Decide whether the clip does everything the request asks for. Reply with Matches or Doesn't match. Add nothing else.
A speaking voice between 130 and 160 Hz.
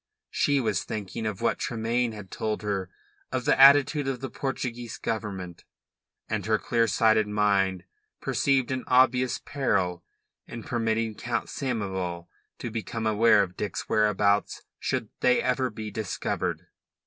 Doesn't match